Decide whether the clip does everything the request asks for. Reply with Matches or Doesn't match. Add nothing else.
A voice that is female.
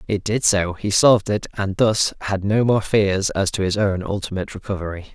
Doesn't match